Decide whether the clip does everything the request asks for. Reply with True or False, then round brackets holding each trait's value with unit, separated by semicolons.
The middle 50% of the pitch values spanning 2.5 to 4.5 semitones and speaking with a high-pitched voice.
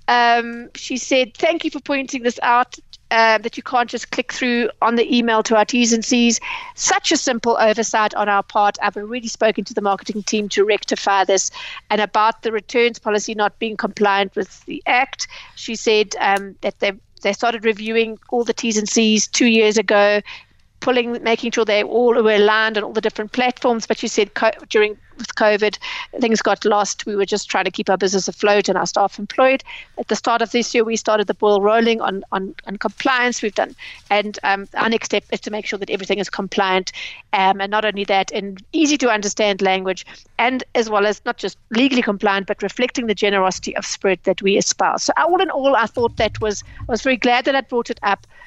True (2.8 semitones; 220 Hz)